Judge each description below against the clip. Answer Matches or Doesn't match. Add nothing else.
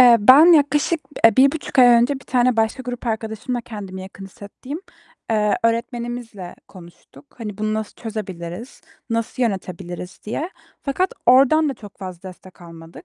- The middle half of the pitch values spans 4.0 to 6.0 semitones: Matches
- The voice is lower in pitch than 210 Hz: Doesn't match